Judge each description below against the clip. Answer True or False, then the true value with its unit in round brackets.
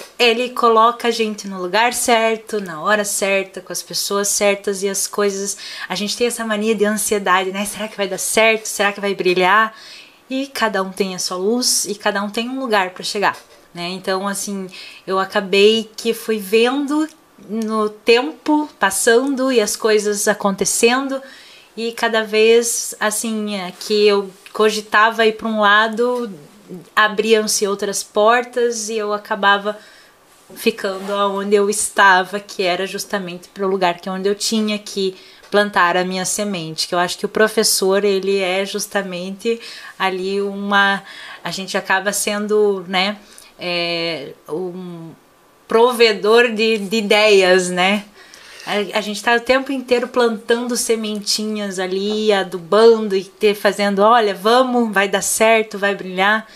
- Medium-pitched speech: False (210 Hz)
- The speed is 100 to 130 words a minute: False (155 wpm)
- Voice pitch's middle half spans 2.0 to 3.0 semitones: True (2.4 semitones)